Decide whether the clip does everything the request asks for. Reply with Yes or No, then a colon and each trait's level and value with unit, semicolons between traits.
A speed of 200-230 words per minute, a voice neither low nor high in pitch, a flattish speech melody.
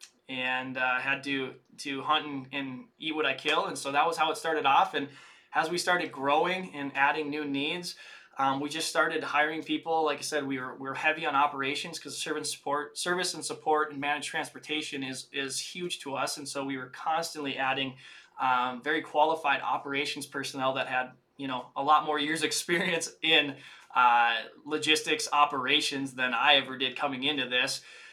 No: average, 190 wpm; medium, 145 Hz; narrow, 2.3 semitones